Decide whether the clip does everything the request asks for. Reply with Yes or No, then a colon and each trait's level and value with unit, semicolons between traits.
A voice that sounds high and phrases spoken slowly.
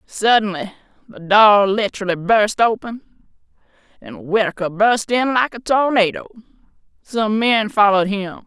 Yes: high, 210 Hz; slow, 120 wpm